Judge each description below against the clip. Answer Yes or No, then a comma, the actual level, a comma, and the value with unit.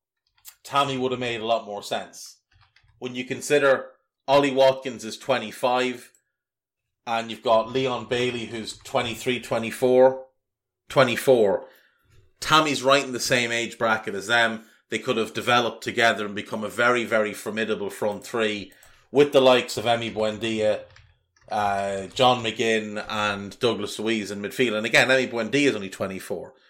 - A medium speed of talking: Yes, average, 150 wpm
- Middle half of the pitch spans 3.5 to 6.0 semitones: No, average, 2.9 semitones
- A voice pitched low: Yes, low, 115 Hz